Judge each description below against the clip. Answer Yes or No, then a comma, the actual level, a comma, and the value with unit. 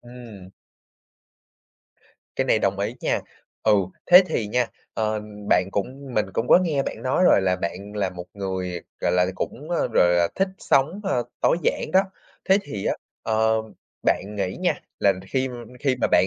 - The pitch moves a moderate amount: No, wide, 5.9 semitones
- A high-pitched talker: No, low, 110 Hz